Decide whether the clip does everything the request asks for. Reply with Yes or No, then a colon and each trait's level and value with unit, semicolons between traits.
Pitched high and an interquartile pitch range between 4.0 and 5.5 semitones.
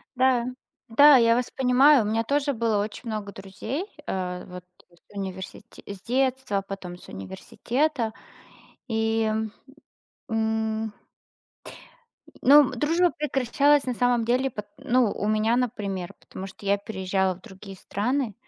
Yes: high, 225 Hz; average, 4.3 semitones